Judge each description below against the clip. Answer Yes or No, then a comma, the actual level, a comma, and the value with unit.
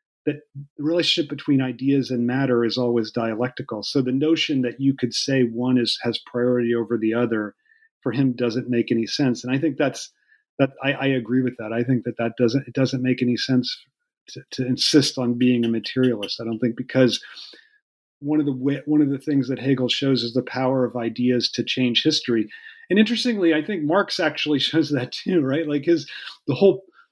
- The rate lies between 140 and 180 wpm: No, fast, 205 wpm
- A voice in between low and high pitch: No, low, 130 Hz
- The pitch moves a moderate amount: Yes, average, 3.3 semitones